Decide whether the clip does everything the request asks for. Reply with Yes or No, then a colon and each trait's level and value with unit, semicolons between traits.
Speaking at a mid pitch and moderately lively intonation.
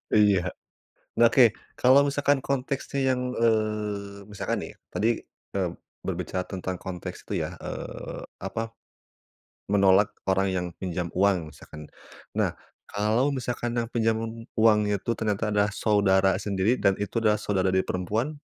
No: low, 105 Hz; average, 3.3 semitones